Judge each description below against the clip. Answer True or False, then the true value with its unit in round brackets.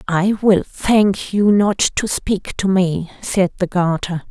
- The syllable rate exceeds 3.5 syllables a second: False (3.4 syllables/s)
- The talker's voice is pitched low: False (190 Hz)